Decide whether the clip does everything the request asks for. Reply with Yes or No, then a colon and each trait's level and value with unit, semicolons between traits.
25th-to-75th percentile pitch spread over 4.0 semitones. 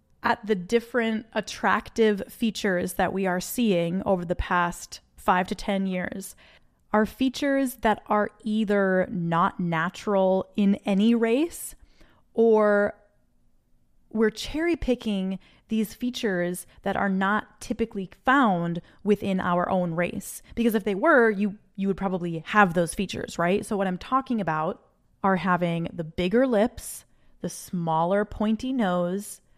No: average, 3.5 semitones